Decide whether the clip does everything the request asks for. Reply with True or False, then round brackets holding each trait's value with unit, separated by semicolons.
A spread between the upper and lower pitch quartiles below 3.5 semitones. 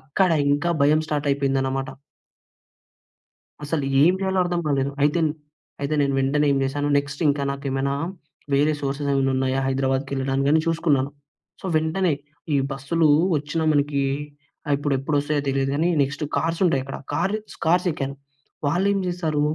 True (2.8 semitones)